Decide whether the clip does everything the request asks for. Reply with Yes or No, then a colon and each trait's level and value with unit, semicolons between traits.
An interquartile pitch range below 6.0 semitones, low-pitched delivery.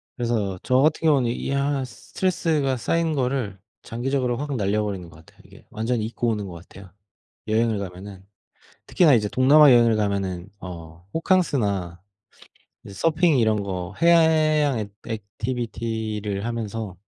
Yes: wide, 5.6 semitones; low, 115 Hz